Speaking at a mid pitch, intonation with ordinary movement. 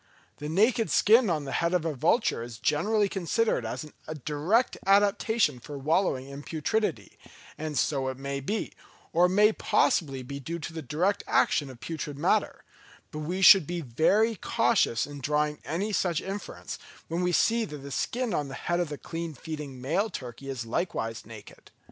No: medium, 160 Hz; wide, 5.9 semitones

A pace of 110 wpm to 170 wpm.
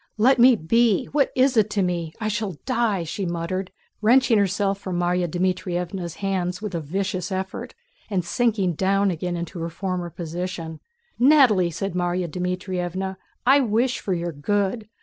Yes: average, 160 wpm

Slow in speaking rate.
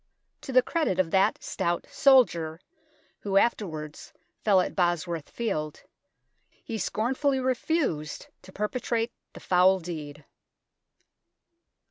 Yes: slow, 105 wpm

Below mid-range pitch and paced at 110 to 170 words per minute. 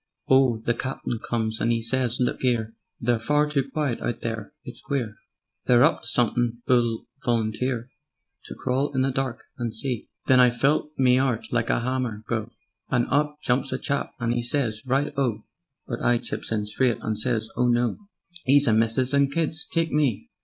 No: low, 125 Hz; average, 195 wpm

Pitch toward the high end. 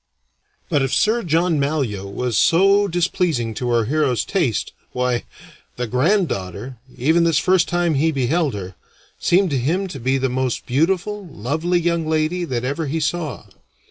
No: medium, 155 Hz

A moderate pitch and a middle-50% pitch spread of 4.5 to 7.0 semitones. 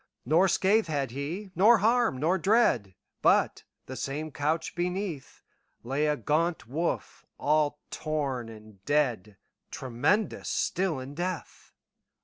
Yes: medium, 155 Hz; wide, 5.6 semitones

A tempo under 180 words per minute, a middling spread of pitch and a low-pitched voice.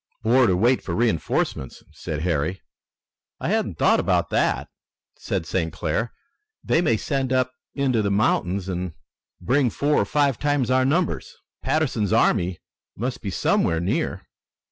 No: average, 145 wpm; wide, 6.3 semitones; low, 115 Hz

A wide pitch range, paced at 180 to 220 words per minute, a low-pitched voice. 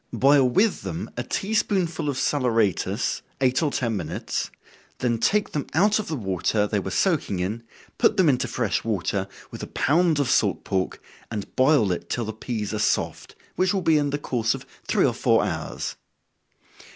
Yes: wide, 7.0 semitones; average, 190 wpm; low, 130 Hz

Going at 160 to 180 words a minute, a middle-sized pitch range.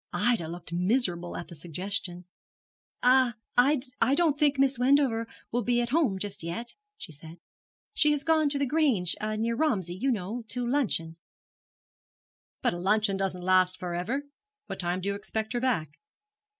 No: average, 165 wpm; wide, 6.4 semitones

